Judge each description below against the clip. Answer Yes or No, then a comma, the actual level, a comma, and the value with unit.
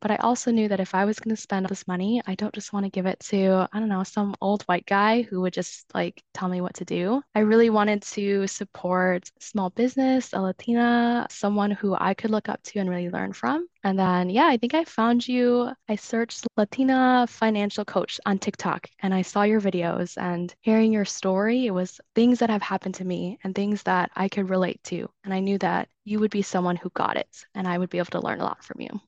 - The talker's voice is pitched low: No, high, 205 Hz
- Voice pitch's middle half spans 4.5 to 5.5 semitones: No, average, 3.2 semitones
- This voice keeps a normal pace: No, fast, 245 wpm